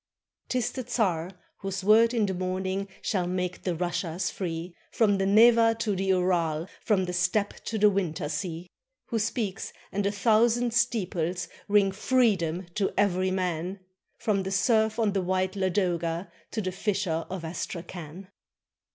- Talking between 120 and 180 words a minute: Yes, average, 160 wpm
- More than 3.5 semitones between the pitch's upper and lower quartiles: No, average, 2.9 semitones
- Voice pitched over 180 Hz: Yes, high, 190 Hz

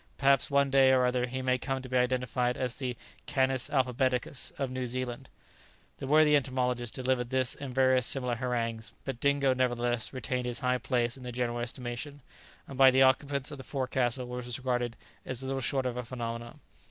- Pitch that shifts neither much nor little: No, narrow, 1.4 semitones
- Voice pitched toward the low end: Yes, low, 130 Hz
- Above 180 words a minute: Yes, average, 190 wpm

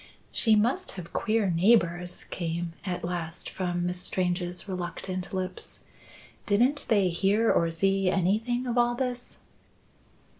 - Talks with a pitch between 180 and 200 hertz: Yes, medium, 185 Hz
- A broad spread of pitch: No, average, 4.1 semitones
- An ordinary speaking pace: No, slow, 125 wpm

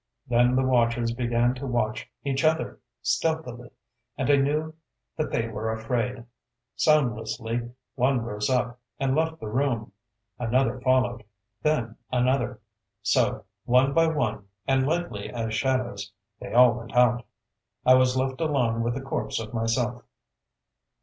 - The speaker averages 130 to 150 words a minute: Yes, average, 140 wpm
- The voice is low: Yes, low, 125 Hz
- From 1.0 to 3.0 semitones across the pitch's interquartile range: Yes, narrow, 2.5 semitones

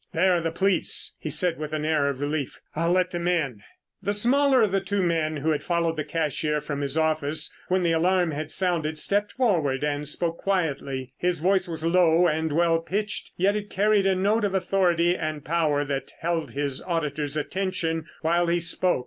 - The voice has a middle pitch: Yes, medium, 165 Hz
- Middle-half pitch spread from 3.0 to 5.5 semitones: Yes, average, 3.3 semitones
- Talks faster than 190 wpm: Yes, average, 200 wpm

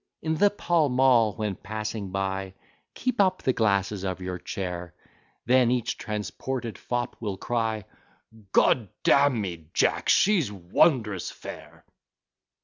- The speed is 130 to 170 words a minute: Yes, average, 140 wpm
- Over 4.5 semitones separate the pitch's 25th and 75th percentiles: Yes, average, 5.0 semitones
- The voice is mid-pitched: No, low, 110 Hz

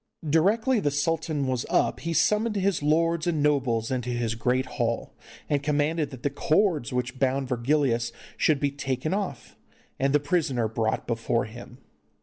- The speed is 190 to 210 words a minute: No, average, 160 wpm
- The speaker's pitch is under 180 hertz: Yes, medium, 140 Hz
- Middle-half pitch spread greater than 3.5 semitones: Yes, average, 4.4 semitones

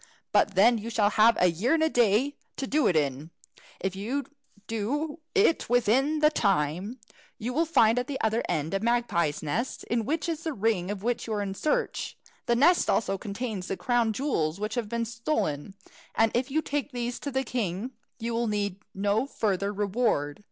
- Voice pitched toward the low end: No, high, 225 Hz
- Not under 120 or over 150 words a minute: No, average, 195 wpm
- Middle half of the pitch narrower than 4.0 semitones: No, average, 4.5 semitones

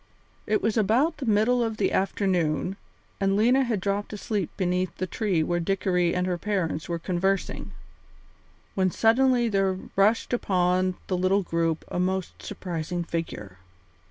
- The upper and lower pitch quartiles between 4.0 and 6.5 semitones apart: No, average, 3.1 semitones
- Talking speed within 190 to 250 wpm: No, average, 150 wpm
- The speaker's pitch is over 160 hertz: Yes, high, 190 Hz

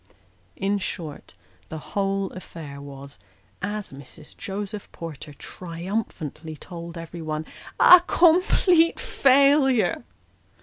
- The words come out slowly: Yes, slow, 90 wpm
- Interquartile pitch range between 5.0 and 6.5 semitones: Yes, wide, 5.4 semitones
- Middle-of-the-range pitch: Yes, medium, 180 Hz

